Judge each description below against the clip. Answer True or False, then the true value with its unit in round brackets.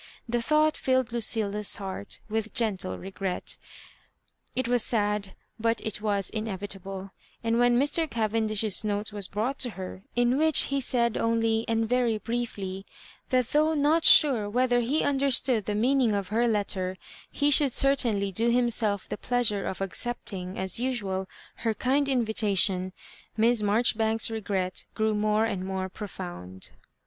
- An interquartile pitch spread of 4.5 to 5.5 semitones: False (3.3 semitones)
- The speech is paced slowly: False (150 wpm)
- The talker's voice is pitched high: True (220 Hz)